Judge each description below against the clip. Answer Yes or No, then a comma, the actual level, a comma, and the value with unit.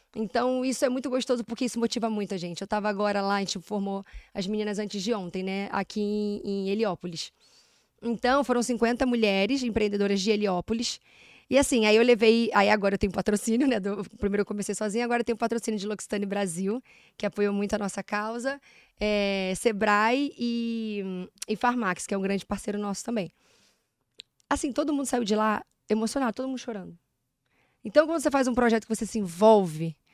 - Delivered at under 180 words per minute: No, fast, 185 wpm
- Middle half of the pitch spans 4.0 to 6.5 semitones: No, average, 2.9 semitones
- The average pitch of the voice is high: Yes, high, 215 Hz